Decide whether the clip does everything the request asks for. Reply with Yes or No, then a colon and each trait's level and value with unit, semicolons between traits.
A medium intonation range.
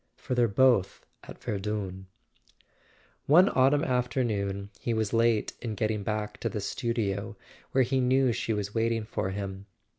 Yes: average, 3.6 semitones